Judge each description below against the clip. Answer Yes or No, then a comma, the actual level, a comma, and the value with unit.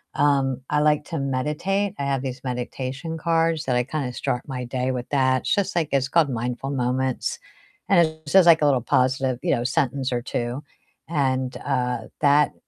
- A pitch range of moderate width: Yes, average, 3.2 semitones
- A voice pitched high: No, low, 135 Hz